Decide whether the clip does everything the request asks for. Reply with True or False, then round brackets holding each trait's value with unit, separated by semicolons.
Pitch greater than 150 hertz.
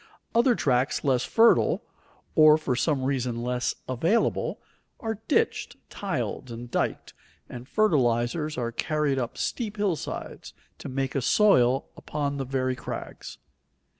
False (135 Hz)